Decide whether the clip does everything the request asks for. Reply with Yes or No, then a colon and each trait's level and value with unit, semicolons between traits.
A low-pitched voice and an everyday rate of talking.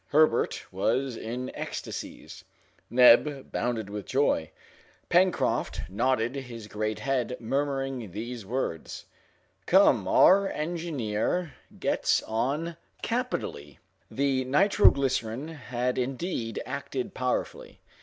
No: low, 130 Hz; slow, 95 wpm